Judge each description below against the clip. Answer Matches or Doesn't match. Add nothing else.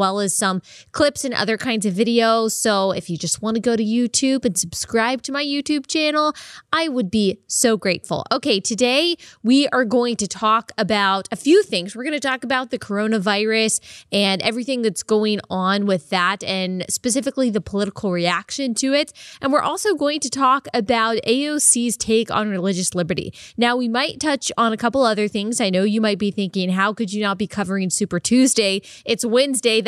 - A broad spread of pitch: Doesn't match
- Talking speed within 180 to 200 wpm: Matches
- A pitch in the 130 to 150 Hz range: Doesn't match